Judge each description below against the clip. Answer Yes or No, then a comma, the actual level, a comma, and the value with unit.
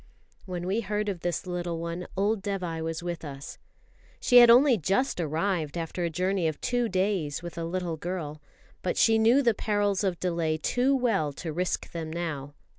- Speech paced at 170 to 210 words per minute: Yes, average, 190 wpm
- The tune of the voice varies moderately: Yes, average, 4.0 semitones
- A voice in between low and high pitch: Yes, medium, 180 Hz